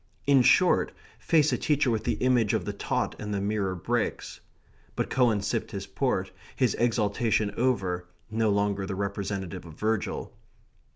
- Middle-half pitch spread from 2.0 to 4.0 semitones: Yes, average, 3.7 semitones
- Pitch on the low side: Yes, low, 105 Hz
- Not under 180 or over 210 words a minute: No, average, 160 wpm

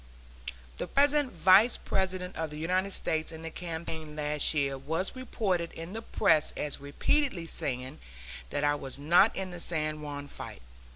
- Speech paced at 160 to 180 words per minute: Yes, average, 165 wpm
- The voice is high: No, medium, 165 Hz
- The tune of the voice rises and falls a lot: No, average, 3.9 semitones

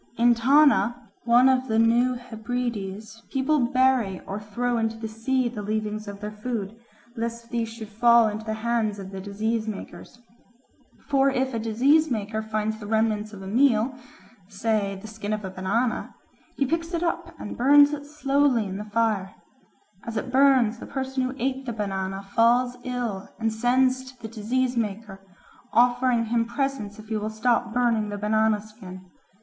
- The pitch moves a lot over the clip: No, average, 3.0 semitones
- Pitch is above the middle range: Yes, high, 230 Hz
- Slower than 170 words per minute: No, average, 175 wpm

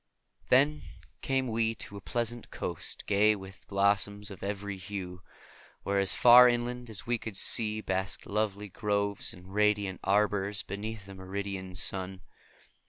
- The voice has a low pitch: Yes, low, 100 Hz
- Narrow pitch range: Yes, narrow, 2.3 semitones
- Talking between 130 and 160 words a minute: Yes, average, 145 wpm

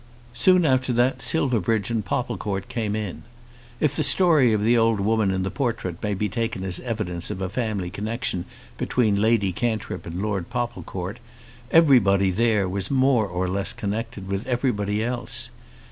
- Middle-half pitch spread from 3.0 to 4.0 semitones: Yes, average, 3.7 semitones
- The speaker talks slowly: No, average, 160 wpm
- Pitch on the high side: No, low, 110 Hz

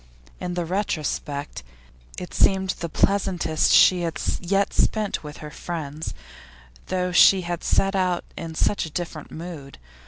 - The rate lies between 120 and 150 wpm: Yes, average, 145 wpm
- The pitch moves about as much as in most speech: Yes, average, 3.1 semitones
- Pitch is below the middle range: No, medium, 175 Hz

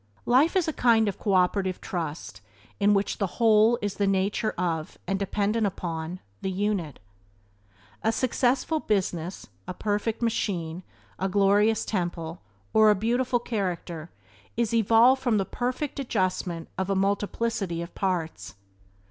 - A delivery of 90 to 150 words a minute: Yes, average, 140 wpm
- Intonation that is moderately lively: Yes, average, 3.7 semitones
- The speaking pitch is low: No, high, 200 Hz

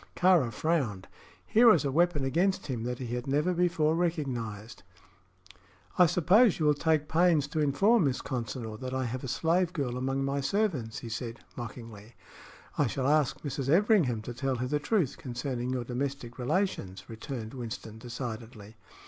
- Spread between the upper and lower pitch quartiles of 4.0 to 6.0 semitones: Yes, average, 5.2 semitones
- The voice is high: No, low, 135 Hz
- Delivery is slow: No, average, 165 wpm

